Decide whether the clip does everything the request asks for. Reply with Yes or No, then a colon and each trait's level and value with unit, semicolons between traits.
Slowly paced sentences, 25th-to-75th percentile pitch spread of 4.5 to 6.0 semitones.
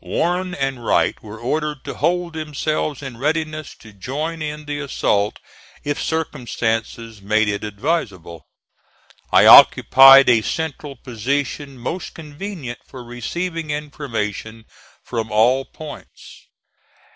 Yes: slow, 115 wpm; average, 5.2 semitones